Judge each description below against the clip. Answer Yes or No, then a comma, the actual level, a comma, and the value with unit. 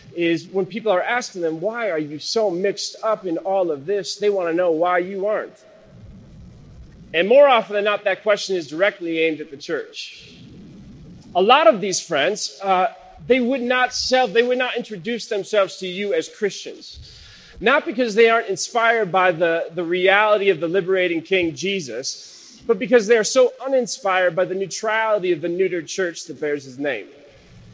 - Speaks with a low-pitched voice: No, high, 195 Hz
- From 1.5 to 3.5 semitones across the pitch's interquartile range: No, average, 4.5 semitones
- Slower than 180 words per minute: No, average, 185 wpm